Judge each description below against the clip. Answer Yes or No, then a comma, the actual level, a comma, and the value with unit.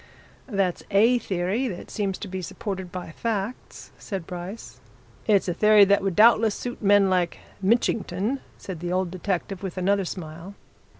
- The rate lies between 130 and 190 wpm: Yes, average, 160 wpm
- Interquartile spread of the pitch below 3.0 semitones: Yes, narrow, 2.6 semitones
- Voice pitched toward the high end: Yes, high, 195 Hz